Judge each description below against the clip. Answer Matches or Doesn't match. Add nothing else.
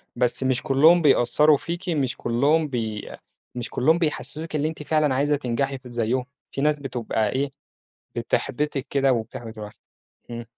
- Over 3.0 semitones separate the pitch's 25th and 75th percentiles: Matches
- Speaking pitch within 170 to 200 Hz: Doesn't match